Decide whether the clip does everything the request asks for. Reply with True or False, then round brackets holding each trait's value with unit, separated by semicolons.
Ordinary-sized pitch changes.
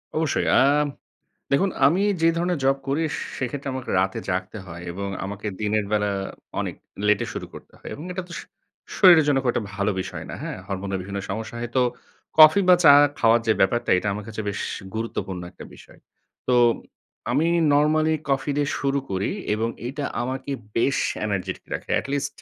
False (6.1 semitones)